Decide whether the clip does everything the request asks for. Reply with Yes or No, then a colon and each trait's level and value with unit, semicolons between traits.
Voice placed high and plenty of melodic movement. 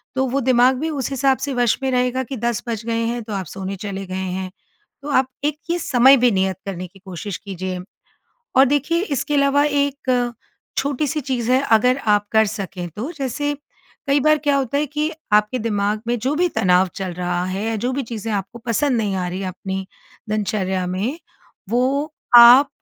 Yes: high, 235 Hz; wide, 5.9 semitones